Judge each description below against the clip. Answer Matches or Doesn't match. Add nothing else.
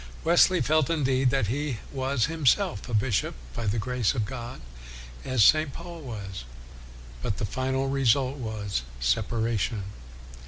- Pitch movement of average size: Matches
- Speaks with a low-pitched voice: Matches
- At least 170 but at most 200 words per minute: Doesn't match